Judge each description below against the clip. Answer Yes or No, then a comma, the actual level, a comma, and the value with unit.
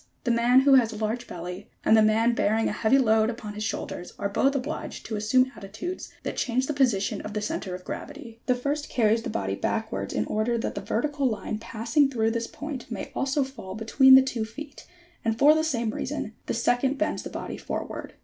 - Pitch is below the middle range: No, high, 230 Hz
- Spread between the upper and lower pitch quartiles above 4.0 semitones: No, average, 3.7 semitones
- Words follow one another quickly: Yes, fast, 220 wpm